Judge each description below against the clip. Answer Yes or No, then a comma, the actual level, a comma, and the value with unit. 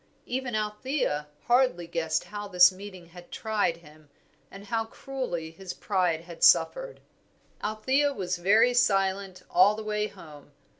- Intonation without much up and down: No, average, 4.3 semitones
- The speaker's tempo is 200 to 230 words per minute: No, average, 140 wpm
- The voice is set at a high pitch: Yes, high, 195 Hz